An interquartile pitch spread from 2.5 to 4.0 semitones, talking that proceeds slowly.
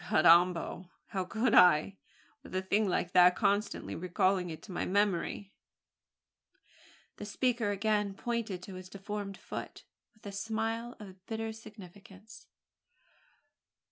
Yes: average, 2.9 semitones; slow, 125 wpm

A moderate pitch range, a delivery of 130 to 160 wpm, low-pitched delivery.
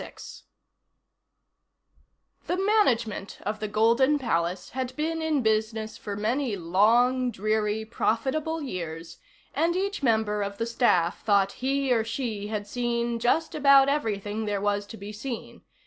No: average, 4.3 semitones; average, 140 wpm; high, 225 Hz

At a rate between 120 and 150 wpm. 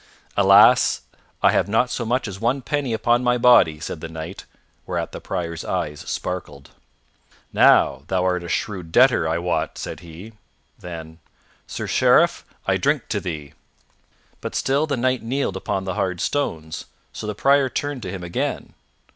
No: average, 165 wpm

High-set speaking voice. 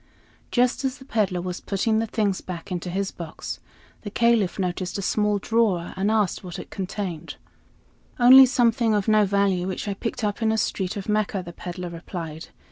Yes: high, 200 Hz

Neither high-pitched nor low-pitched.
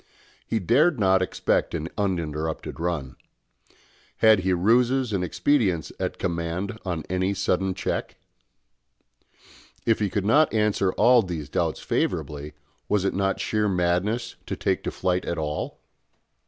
No: very low, 95 Hz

